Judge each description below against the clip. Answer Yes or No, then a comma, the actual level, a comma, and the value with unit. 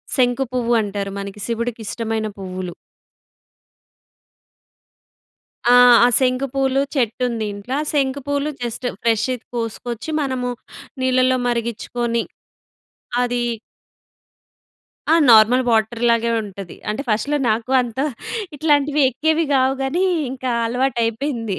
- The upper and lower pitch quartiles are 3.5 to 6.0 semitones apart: No, average, 2.9 semitones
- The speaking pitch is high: Yes, high, 240 Hz